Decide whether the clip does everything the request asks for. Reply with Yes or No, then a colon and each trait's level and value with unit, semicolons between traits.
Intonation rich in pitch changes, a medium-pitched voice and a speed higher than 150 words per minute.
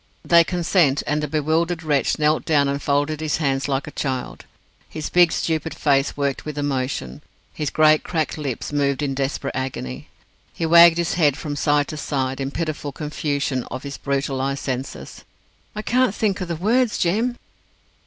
No: average, 3.0 semitones; medium, 150 Hz; average, 175 wpm